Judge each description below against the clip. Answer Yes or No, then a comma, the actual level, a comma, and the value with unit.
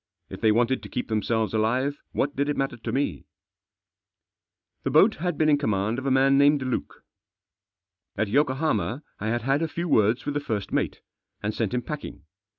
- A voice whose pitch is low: Yes, low, 130 Hz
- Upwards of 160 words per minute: Yes, average, 195 wpm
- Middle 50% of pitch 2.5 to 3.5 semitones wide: No, average, 4.5 semitones